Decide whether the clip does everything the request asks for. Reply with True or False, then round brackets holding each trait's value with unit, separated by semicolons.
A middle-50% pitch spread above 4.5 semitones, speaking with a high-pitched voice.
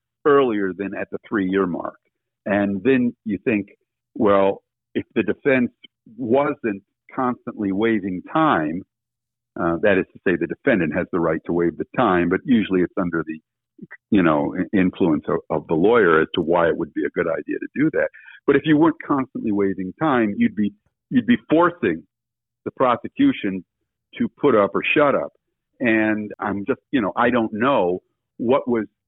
False (5.5 semitones; 110 Hz)